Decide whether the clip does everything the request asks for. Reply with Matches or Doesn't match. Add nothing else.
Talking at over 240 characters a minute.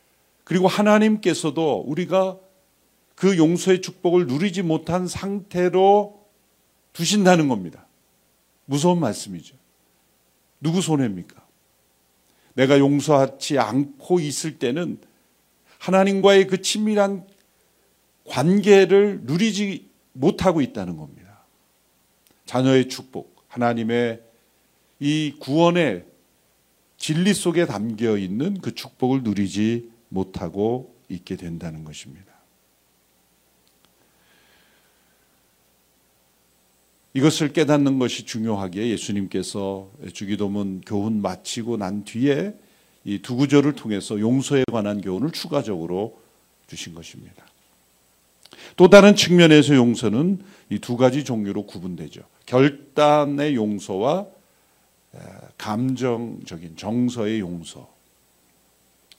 Doesn't match